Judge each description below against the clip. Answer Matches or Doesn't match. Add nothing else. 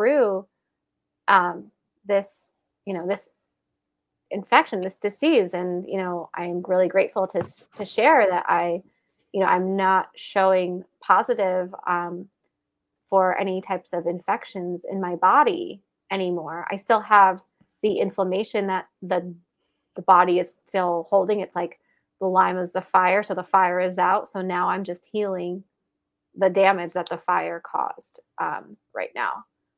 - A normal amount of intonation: Doesn't match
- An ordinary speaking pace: Matches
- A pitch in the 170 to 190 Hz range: Matches